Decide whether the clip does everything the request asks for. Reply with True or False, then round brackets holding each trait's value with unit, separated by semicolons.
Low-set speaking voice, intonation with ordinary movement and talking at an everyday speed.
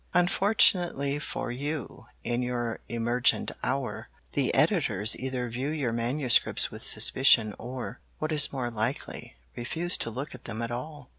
True (125 Hz; 3.6 semitones; 145 wpm)